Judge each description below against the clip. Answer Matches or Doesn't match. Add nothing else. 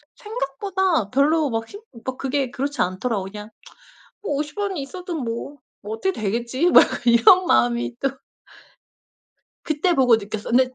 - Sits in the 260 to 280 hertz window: Matches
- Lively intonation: Matches